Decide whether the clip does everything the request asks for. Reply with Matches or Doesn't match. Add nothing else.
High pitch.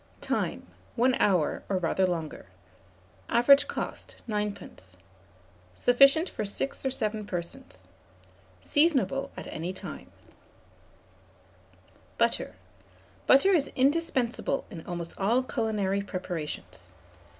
Matches